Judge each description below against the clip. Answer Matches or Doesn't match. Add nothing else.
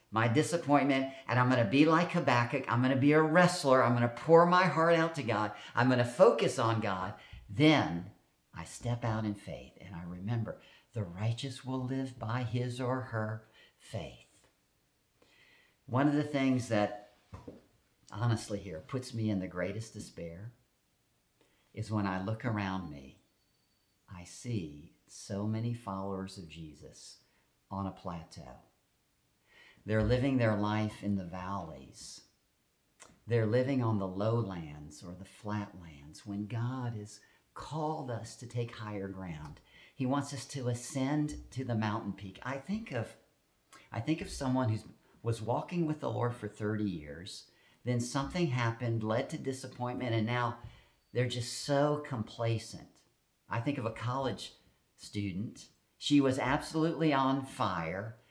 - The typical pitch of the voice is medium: Doesn't match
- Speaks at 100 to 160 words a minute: Matches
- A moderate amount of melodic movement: Matches